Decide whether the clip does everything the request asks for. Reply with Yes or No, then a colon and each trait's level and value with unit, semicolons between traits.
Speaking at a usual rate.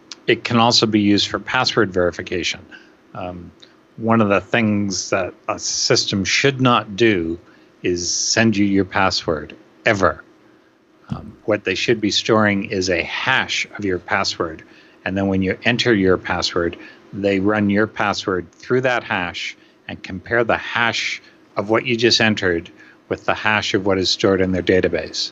Yes: average, 165 wpm